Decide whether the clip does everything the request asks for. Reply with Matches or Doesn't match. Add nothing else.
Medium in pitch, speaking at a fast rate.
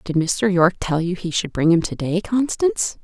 Matches